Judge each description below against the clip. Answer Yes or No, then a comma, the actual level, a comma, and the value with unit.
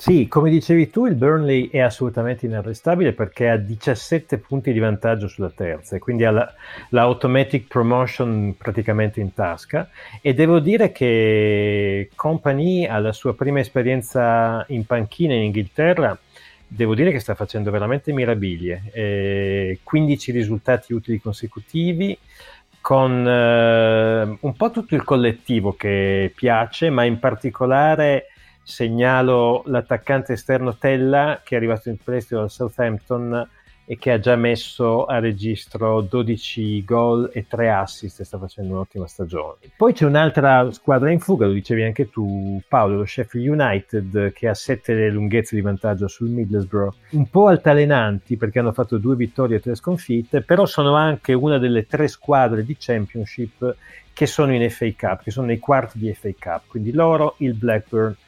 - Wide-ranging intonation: No, average, 3.8 semitones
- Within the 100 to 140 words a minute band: No, average, 155 wpm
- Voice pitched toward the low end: Yes, low, 120 Hz